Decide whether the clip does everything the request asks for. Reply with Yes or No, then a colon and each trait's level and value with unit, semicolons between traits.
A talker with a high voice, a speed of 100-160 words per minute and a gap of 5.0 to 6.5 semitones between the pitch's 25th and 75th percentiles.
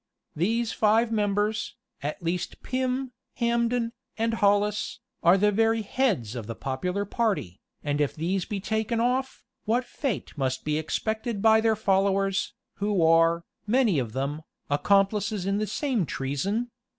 Yes: high, 205 Hz; average, 145 wpm; average, 5.3 semitones